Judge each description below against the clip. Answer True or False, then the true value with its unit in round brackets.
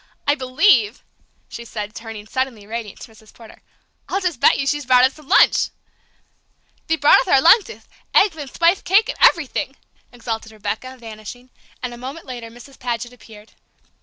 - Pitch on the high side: True (250 Hz)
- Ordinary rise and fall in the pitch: True (4.4 semitones)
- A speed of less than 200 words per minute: True (170 wpm)